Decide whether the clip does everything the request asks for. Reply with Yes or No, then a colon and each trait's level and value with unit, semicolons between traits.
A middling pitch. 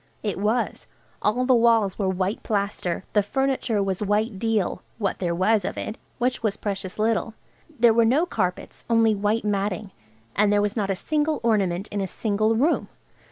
No: high, 210 Hz